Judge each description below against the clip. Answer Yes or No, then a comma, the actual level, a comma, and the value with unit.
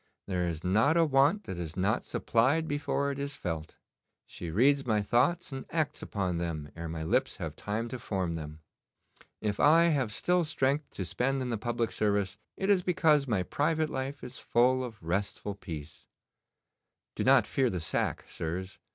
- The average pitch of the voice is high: No, low, 115 Hz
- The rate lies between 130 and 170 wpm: No, average, 180 wpm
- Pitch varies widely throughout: Yes, wide, 7.5 semitones